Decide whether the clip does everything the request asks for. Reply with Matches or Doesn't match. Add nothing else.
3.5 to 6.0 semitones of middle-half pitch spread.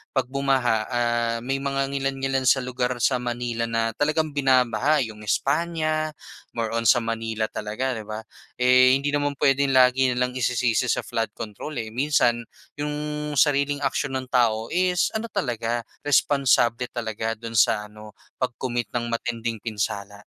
Doesn't match